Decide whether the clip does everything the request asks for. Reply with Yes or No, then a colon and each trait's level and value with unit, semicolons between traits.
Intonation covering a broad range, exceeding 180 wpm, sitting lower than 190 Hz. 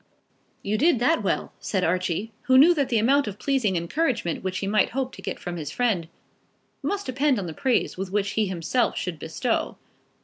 No: wide, 6.2 semitones; average, 195 wpm; high, 215 Hz